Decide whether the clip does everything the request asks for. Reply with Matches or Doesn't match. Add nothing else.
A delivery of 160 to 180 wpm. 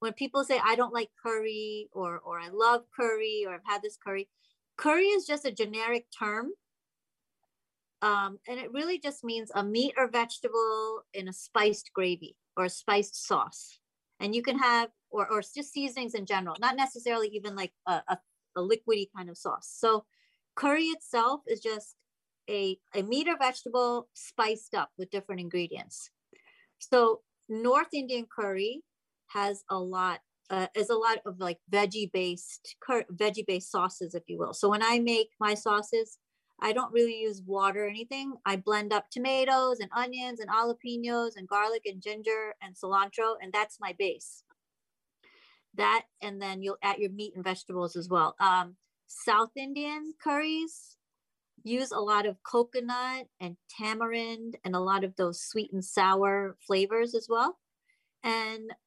Matches